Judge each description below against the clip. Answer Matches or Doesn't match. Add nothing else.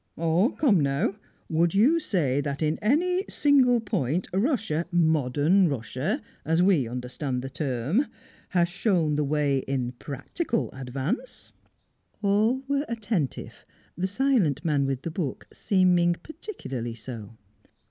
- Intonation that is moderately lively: Doesn't match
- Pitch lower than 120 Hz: Doesn't match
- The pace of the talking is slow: Matches